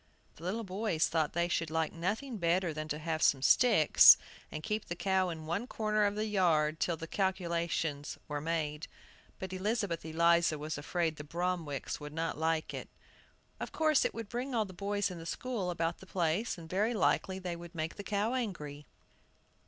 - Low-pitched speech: No, medium, 175 Hz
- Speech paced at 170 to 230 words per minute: Yes, average, 190 wpm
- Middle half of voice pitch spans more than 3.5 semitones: Yes, average, 4.1 semitones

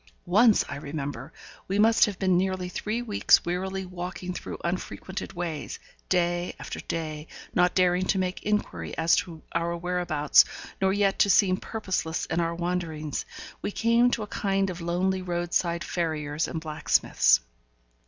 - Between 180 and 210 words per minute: No, average, 155 wpm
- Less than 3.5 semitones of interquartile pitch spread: Yes, narrow, 2.4 semitones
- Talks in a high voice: No, medium, 180 Hz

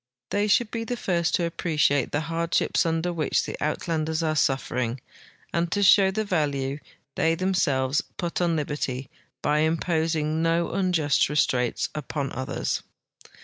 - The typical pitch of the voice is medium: Yes, medium, 160 Hz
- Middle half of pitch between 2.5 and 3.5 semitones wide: Yes, average, 3.0 semitones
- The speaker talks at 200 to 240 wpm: No, average, 145 wpm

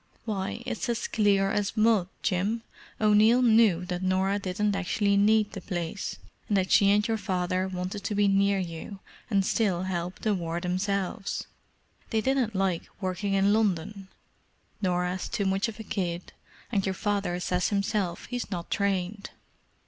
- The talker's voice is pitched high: Yes, high, 195 Hz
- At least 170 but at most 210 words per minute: No, average, 155 wpm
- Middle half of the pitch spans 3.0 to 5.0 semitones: No, narrow, 2.4 semitones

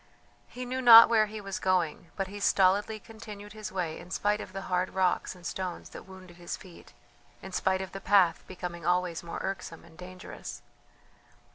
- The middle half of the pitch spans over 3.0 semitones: No, narrow, 2.4 semitones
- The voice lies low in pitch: No, high, 190 Hz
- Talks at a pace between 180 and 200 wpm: Yes, average, 185 wpm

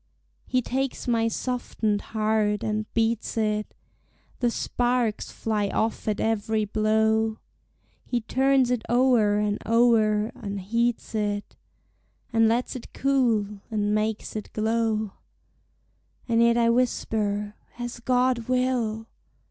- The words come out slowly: Yes, slow, 120 wpm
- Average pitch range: No, narrow, 2.2 semitones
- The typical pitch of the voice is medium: No, high, 225 Hz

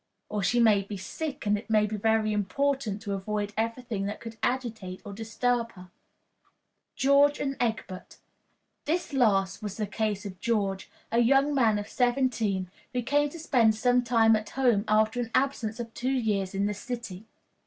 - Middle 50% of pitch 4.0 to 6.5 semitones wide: No, average, 3.2 semitones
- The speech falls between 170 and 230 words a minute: Yes, average, 180 wpm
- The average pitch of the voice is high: Yes, high, 220 Hz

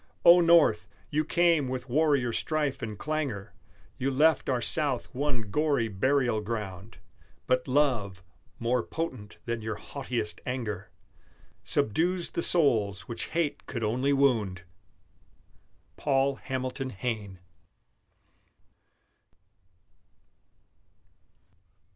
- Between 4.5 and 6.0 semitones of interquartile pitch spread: Yes, average, 5.1 semitones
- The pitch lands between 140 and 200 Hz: No, low, 130 Hz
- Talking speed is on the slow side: Yes, slow, 100 wpm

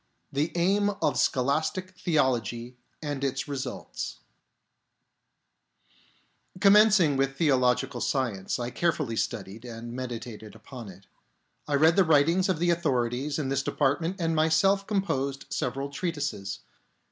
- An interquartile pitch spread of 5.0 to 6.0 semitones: Yes, average, 5.3 semitones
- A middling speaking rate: No, slow, 125 wpm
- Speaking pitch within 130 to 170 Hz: Yes, medium, 140 Hz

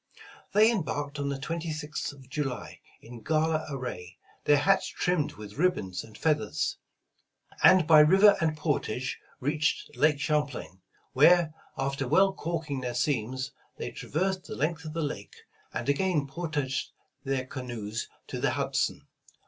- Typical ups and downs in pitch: Yes, average, 3.8 semitones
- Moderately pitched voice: Yes, medium, 145 Hz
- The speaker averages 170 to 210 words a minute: No, average, 140 wpm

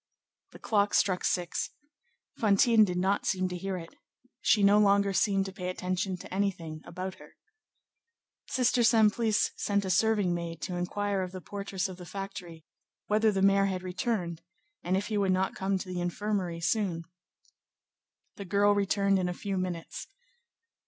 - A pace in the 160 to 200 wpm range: Yes, average, 165 wpm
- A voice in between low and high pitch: No, high, 195 Hz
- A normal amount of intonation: No, narrow, 2.0 semitones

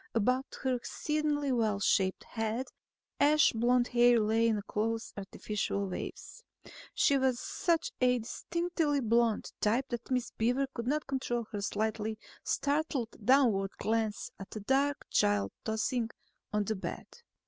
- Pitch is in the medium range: No, high, 235 Hz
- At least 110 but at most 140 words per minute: Yes, slow, 135 wpm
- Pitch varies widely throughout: No, average, 3.7 semitones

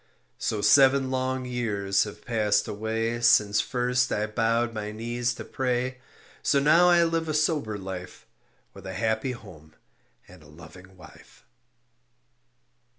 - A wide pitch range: No, average, 3.9 semitones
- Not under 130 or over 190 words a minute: Yes, average, 140 wpm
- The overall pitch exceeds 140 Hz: No, low, 115 Hz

